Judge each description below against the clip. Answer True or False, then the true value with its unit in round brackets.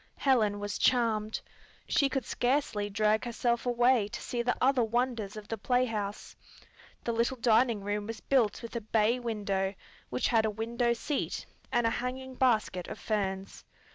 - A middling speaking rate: True (165 wpm)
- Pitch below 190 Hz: False (230 Hz)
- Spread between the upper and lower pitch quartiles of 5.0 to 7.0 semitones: False (2.9 semitones)